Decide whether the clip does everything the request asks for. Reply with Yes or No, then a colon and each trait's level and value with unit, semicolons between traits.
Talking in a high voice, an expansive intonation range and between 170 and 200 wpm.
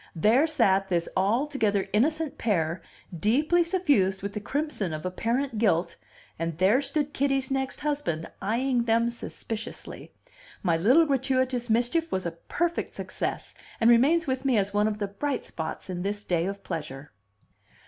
No: high, 225 Hz; wide, 6.3 semitones; average, 155 wpm